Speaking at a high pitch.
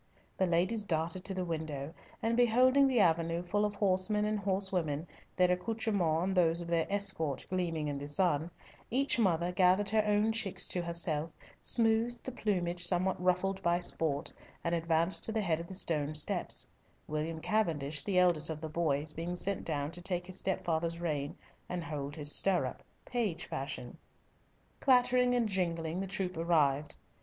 No: medium, 175 Hz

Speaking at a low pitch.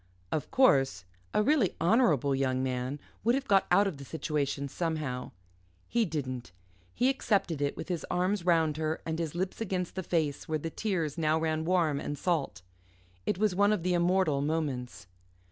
No: medium, 160 Hz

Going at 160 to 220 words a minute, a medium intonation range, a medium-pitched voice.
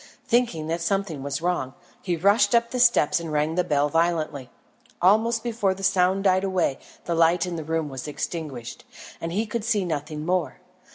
Yes: average, 185 wpm; average, 4.1 semitones; medium, 175 Hz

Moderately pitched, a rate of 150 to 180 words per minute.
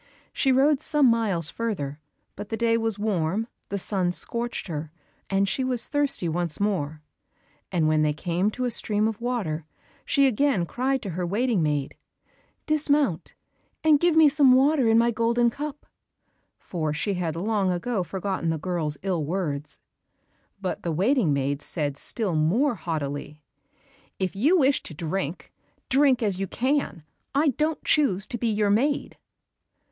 No: high, 205 Hz; average, 160 wpm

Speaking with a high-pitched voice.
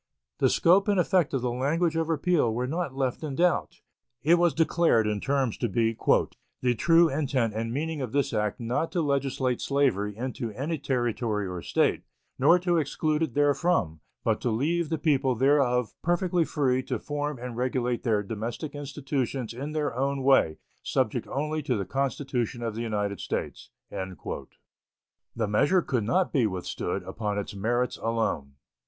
No: low, 130 Hz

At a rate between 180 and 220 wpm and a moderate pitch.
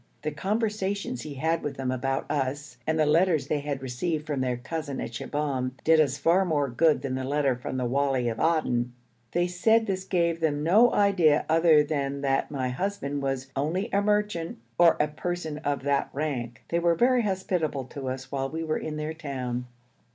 Yes: average, 195 wpm; medium, 150 Hz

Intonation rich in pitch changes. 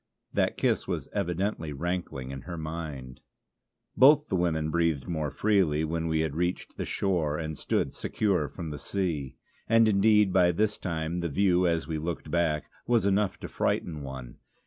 No: average, 3.6 semitones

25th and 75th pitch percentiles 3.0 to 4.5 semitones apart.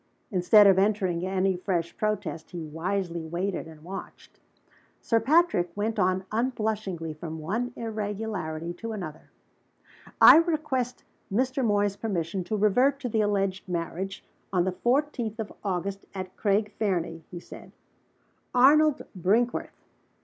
Yes: average, 4.0 semitones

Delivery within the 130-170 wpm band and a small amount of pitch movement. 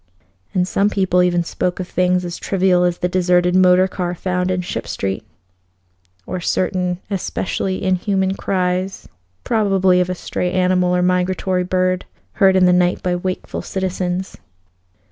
Yes: average, 150 wpm; narrow, 0.8 semitones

